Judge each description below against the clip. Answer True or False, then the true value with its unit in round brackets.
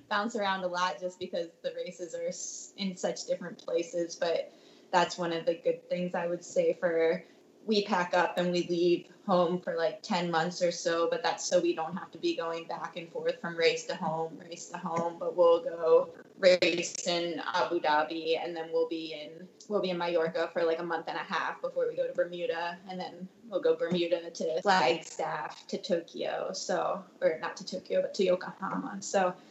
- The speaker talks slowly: False (205 wpm)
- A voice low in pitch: False (180 Hz)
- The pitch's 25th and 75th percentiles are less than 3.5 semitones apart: False (4.6 semitones)